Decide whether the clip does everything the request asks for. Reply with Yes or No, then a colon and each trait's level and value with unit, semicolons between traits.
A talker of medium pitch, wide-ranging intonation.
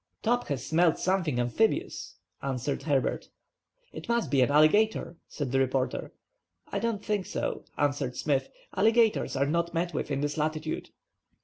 Yes: medium, 155 Hz; wide, 5.9 semitones